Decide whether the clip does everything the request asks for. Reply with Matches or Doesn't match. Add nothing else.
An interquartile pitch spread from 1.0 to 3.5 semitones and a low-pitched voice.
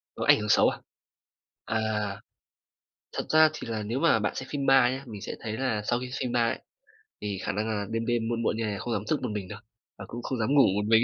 Matches